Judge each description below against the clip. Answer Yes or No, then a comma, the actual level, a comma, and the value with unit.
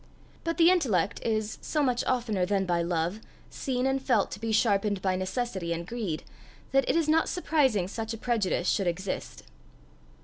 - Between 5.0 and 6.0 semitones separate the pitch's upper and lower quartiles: Yes, wide, 5.5 semitones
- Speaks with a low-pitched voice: No, high, 215 Hz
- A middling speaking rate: Yes, average, 175 wpm